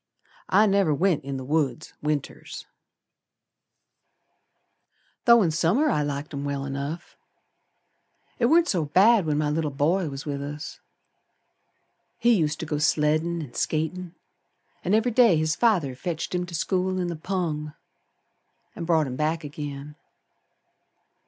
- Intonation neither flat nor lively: Yes, average, 3.8 semitones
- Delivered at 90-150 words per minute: Yes, average, 145 wpm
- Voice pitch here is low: No, medium, 160 Hz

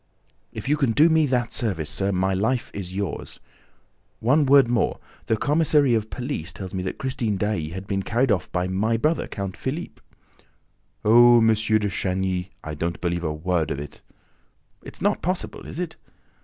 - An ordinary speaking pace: Yes, average, 180 wpm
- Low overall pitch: Yes, low, 110 Hz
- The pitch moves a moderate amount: No, wide, 5.9 semitones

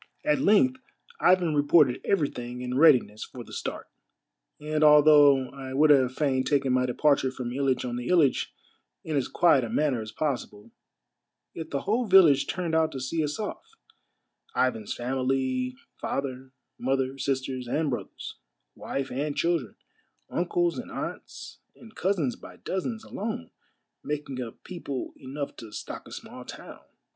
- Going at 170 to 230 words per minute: No, average, 150 wpm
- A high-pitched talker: No, medium, 140 Hz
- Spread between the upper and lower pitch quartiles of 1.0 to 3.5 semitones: No, average, 3.9 semitones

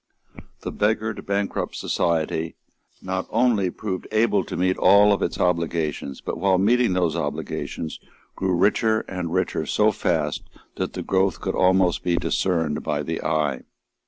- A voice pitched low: Yes, very low, 90 Hz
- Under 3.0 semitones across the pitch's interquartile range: No, average, 3.6 semitones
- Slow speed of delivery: No, average, 150 wpm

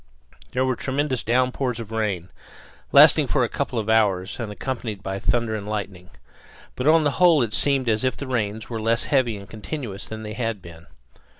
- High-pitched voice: No, low, 110 Hz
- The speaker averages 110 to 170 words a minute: No, average, 195 wpm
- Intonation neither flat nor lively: Yes, average, 3.8 semitones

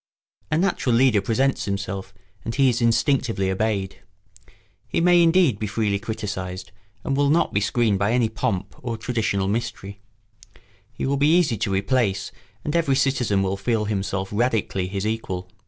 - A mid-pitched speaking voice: No, low, 110 Hz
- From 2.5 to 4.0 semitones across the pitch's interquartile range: No, average, 5.0 semitones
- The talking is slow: No, average, 160 wpm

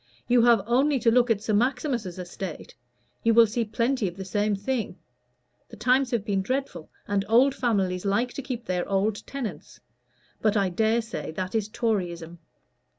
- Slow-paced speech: No, average, 175 wpm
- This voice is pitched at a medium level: No, high, 220 Hz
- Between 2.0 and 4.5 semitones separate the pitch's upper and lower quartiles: Yes, average, 3.8 semitones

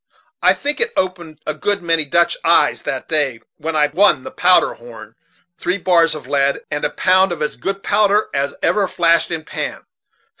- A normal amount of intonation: Yes, average, 4.0 semitones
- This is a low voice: No, medium, 165 Hz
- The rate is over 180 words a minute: Yes, average, 190 wpm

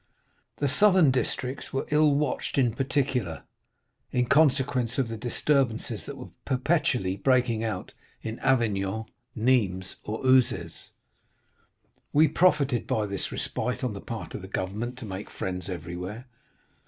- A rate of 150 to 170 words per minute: No, slow, 135 wpm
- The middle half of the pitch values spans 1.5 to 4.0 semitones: No, average, 4.6 semitones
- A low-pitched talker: Yes, low, 125 Hz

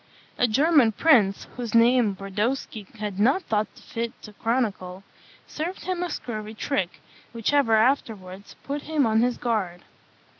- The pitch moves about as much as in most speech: Yes, average, 4.5 semitones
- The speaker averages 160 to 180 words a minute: No, average, 145 wpm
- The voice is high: Yes, high, 230 Hz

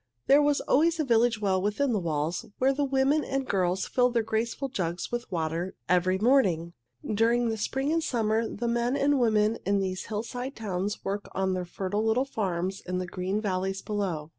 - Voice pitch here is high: Yes, high, 215 Hz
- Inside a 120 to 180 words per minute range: No, average, 190 wpm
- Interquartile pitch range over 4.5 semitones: Yes, average, 5.0 semitones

